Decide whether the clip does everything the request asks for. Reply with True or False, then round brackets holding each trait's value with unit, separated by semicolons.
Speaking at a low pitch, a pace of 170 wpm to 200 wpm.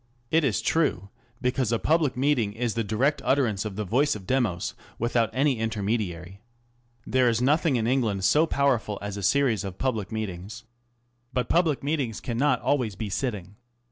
True (115 Hz; 175 wpm)